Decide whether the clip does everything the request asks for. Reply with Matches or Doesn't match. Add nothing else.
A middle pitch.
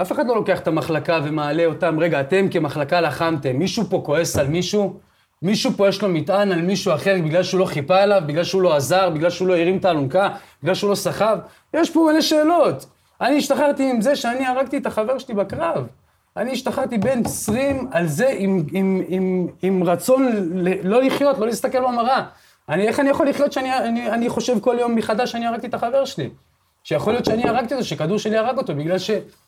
Doesn't match